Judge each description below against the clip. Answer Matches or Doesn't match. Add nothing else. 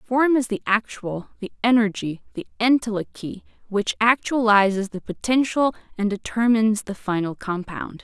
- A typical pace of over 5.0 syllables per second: Doesn't match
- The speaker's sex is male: Doesn't match